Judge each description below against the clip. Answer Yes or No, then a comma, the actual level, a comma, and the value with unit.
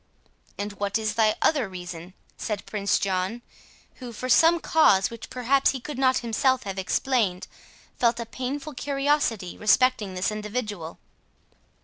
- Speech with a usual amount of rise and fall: Yes, average, 4.5 semitones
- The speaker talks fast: No, average, 140 wpm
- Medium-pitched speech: No, high, 225 Hz